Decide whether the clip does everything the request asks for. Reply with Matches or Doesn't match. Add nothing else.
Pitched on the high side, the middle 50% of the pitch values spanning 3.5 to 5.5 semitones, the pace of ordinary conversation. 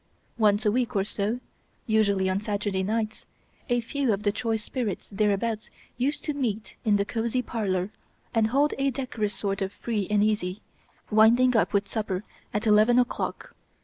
Doesn't match